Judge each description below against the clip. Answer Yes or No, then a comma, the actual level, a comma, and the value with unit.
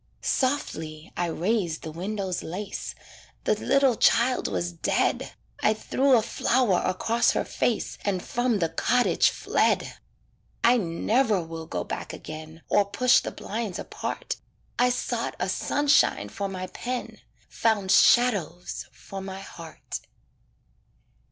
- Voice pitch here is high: Yes, high, 200 Hz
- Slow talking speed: Yes, slow, 130 wpm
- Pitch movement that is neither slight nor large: No, wide, 6.0 semitones